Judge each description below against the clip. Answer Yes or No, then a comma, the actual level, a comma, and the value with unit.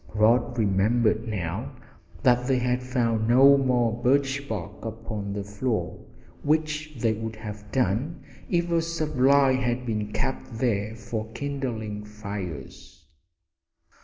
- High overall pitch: No, low, 120 Hz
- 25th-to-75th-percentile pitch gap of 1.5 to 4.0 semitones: Yes, average, 3.7 semitones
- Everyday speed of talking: No, slow, 125 wpm